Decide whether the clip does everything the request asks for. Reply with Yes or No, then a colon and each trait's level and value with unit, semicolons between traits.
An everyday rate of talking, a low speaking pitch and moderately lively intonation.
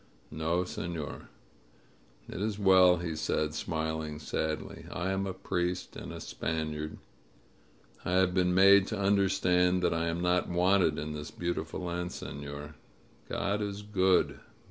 Yes: average, 145 wpm; very low, 90 Hz; average, 3.2 semitones